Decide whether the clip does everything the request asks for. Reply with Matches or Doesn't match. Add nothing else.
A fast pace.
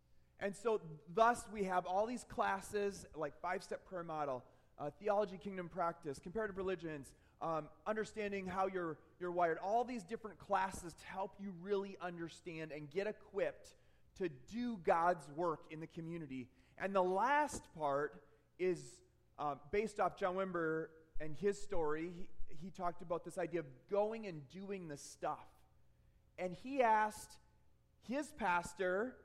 Doesn't match